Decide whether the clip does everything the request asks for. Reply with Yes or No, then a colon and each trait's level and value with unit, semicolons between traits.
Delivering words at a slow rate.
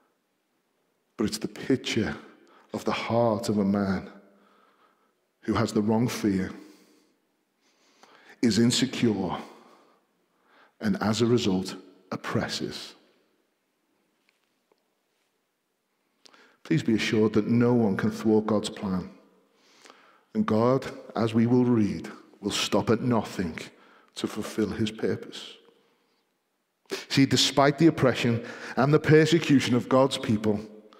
Yes: slow, 110 wpm